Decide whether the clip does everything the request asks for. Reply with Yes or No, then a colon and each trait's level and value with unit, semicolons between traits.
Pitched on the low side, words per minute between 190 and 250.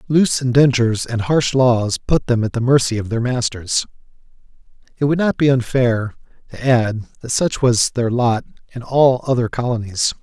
No: low, 125 Hz; average, 170 wpm